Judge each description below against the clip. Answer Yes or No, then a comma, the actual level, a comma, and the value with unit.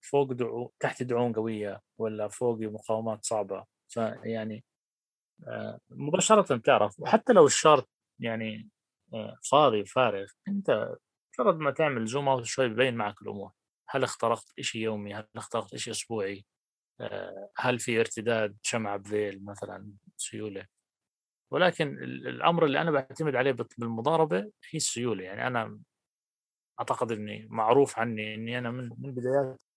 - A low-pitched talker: Yes, low, 115 Hz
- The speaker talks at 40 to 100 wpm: No, average, 125 wpm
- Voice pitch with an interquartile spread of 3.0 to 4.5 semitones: Yes, average, 3.7 semitones